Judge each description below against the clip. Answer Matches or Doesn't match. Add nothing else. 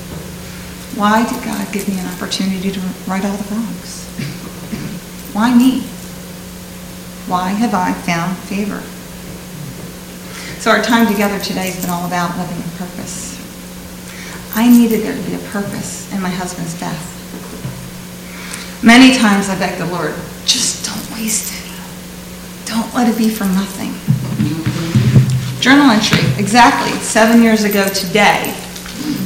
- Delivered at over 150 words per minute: Doesn't match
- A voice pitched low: Doesn't match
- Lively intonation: Doesn't match